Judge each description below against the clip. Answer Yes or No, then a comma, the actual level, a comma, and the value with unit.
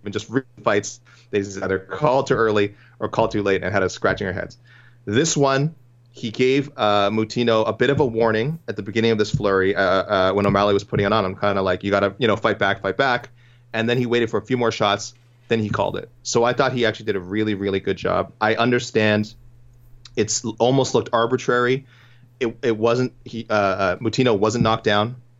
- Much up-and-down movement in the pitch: No, average, 2.7 semitones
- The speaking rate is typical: No, fast, 225 wpm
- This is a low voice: Yes, low, 115 Hz